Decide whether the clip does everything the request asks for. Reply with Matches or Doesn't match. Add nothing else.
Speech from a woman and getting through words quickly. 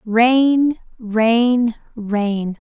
Doesn't match